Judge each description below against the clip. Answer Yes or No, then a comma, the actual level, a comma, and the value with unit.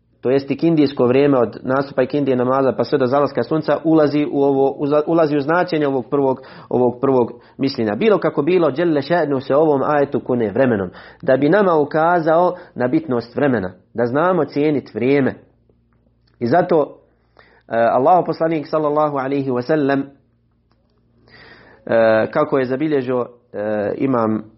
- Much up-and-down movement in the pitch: No, average, 3.6 semitones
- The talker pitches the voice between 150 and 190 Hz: No, medium, 140 Hz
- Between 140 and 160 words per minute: Yes, average, 150 wpm